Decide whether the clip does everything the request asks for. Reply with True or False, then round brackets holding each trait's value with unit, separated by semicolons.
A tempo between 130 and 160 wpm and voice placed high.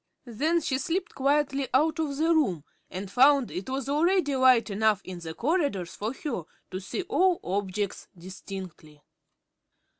True (150 wpm; 260 Hz)